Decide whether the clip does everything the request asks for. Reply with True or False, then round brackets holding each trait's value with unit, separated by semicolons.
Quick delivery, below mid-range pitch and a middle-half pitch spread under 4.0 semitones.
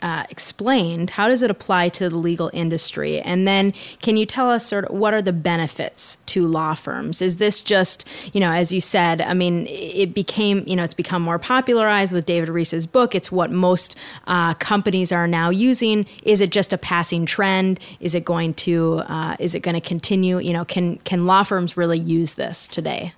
False (210 wpm; 180 Hz; 2.8 semitones)